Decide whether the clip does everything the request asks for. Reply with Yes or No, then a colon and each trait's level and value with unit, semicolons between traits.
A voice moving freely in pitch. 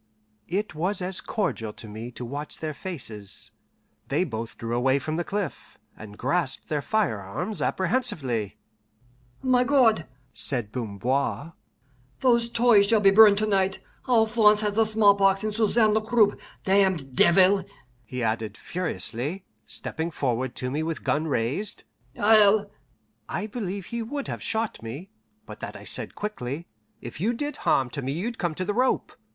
Yes: wide, 8.4 semitones